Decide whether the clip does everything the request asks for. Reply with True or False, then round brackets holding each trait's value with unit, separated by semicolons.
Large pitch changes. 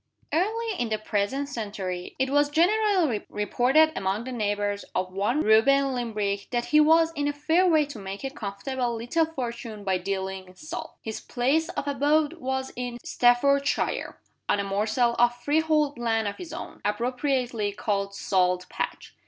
True (6.0 semitones)